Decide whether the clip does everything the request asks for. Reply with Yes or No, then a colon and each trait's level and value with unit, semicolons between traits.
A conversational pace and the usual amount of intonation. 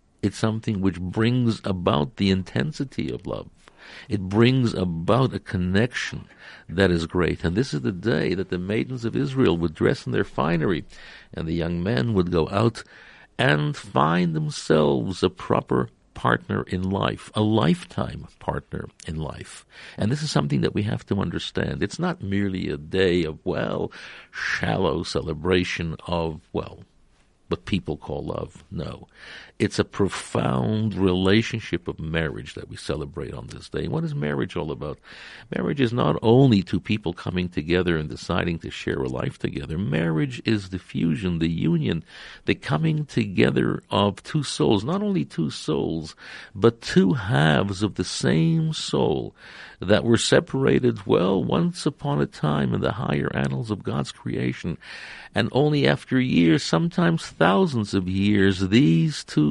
No: average, 160 wpm; wide, 5.9 semitones